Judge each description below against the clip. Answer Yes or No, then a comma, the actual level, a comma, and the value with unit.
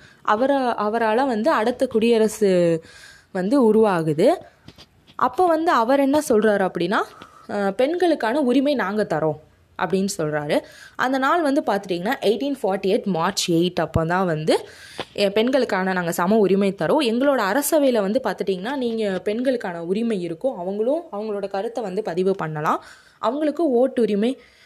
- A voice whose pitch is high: Yes, high, 215 Hz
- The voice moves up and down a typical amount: No, wide, 5.8 semitones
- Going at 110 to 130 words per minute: Yes, average, 125 wpm